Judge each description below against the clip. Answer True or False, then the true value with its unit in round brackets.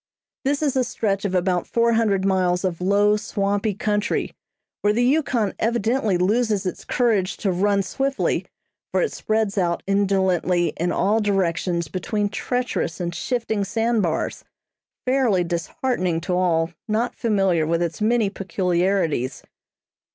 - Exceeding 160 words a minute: False (140 wpm)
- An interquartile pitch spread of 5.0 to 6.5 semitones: False (3.8 semitones)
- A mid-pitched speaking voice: False (200 Hz)